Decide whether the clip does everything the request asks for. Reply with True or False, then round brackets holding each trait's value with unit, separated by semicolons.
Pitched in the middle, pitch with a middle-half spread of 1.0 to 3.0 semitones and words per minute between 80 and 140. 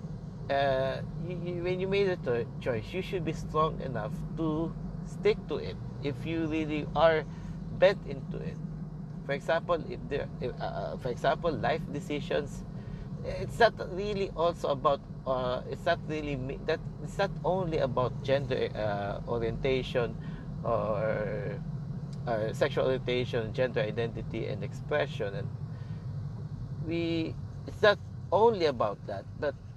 False (155 Hz; 3.9 semitones; 135 wpm)